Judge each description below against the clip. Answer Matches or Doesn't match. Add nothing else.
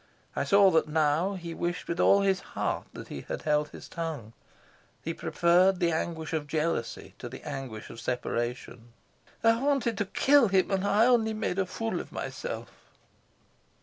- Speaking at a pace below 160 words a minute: Doesn't match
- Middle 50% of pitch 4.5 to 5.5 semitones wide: Matches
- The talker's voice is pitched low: Doesn't match